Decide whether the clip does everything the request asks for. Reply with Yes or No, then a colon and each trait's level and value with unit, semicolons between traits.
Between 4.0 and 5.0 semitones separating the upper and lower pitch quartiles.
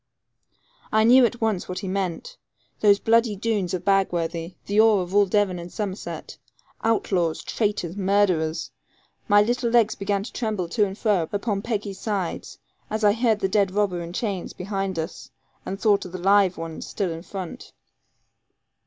No: average, 2.8 semitones